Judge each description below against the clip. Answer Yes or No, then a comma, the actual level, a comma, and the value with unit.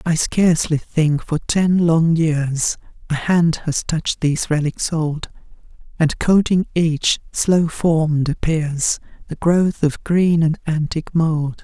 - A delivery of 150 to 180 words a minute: No, average, 140 wpm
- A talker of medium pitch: Yes, medium, 160 Hz